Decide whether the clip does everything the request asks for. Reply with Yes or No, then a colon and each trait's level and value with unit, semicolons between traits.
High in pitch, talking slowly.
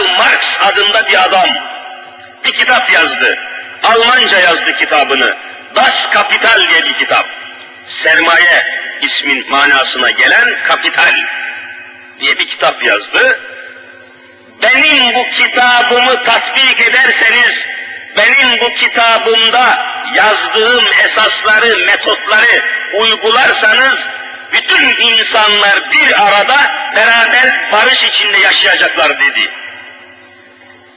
Yes: very high, 380 Hz; slow, 85 wpm